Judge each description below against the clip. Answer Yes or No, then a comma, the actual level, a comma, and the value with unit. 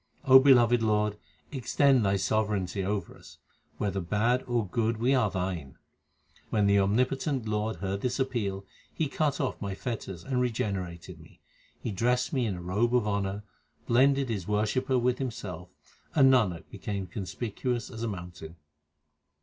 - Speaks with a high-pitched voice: No, low, 110 Hz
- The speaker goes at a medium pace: Yes, average, 160 wpm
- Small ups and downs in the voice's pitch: No, average, 4.3 semitones